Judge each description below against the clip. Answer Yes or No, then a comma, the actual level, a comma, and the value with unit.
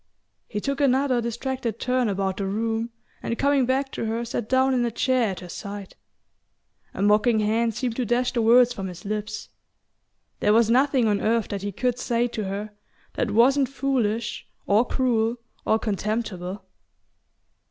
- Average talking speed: Yes, average, 170 wpm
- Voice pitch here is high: Yes, high, 230 Hz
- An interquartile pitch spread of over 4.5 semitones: No, average, 3.1 semitones